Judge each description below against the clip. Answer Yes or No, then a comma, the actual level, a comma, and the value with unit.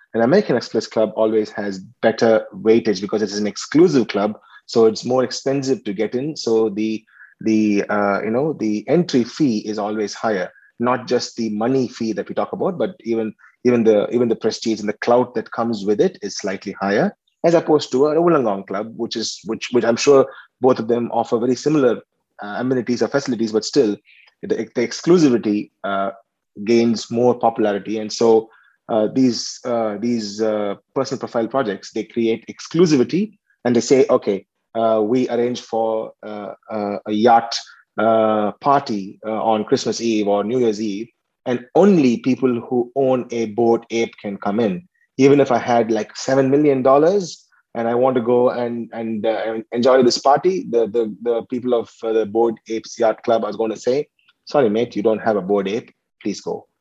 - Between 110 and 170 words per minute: No, average, 190 wpm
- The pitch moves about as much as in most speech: No, narrow, 2.3 semitones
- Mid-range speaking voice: No, low, 115 Hz